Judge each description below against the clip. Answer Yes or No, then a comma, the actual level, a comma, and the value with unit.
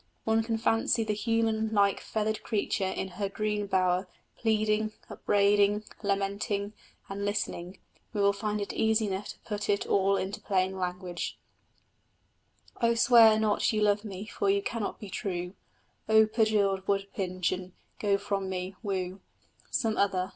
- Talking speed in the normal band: Yes, average, 150 wpm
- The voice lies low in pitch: No, high, 200 Hz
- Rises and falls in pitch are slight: Yes, narrow, 2.0 semitones